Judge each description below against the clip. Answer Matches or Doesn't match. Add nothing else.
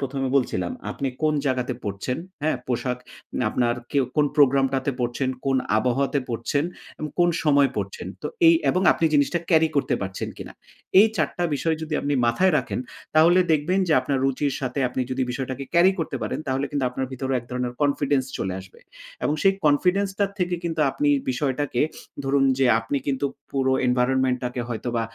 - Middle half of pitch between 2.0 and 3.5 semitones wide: Matches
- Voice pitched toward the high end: Doesn't match